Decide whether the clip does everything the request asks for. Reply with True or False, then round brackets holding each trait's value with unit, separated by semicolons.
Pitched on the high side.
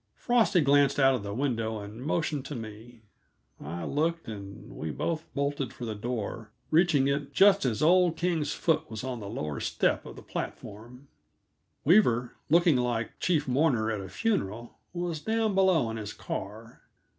False (130 Hz)